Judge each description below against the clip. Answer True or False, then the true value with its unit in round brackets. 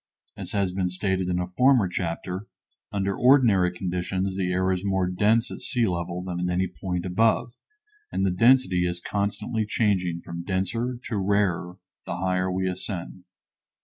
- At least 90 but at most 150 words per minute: False (165 wpm)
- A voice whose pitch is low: True (95 Hz)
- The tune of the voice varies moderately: False (2.3 semitones)